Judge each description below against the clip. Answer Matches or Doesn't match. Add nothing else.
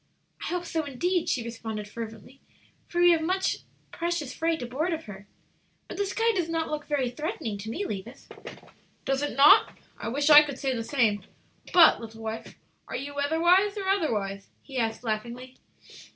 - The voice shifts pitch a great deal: Matches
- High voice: Matches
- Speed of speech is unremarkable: Matches